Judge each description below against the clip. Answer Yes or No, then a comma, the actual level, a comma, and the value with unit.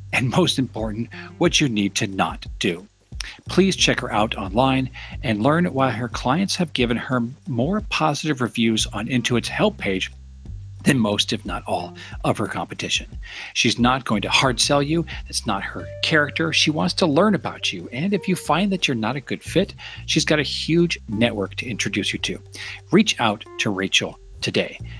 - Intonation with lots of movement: Yes, wide, 6.5 semitones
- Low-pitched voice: Yes, low, 120 Hz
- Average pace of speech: Yes, average, 185 wpm